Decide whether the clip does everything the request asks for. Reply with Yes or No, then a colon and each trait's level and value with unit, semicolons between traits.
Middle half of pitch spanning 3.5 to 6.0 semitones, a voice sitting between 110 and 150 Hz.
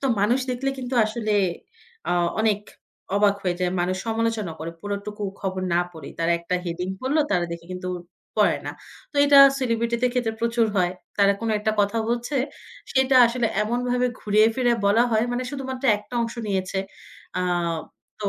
No: average, 4.3 semitones; high, 220 Hz